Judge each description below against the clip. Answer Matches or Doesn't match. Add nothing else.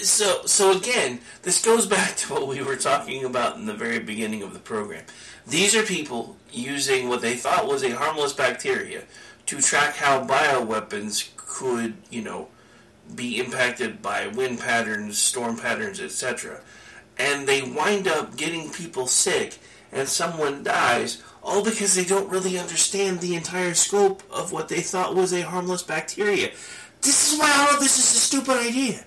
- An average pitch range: Doesn't match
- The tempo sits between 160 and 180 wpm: Matches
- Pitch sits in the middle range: Matches